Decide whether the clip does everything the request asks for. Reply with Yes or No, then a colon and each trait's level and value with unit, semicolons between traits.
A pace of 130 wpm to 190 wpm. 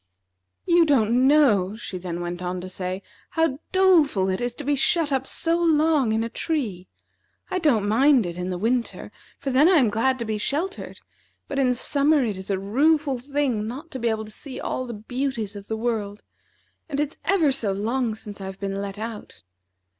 No: average, 200 wpm